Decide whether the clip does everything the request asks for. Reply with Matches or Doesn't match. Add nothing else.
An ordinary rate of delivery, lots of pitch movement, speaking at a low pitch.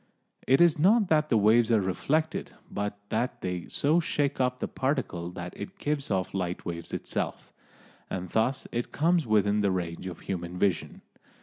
Matches